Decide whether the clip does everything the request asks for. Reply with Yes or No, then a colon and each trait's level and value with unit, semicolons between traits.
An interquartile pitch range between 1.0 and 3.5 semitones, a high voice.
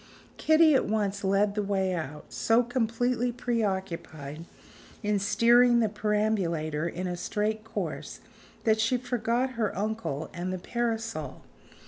No: average, 4.0 semitones; high, 210 Hz